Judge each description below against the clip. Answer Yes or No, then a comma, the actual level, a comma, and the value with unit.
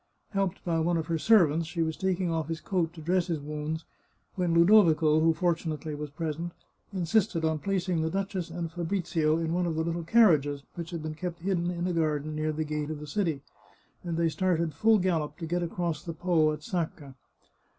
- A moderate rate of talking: No, fast, 210 wpm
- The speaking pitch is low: No, medium, 165 Hz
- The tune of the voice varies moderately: No, narrow, 2.2 semitones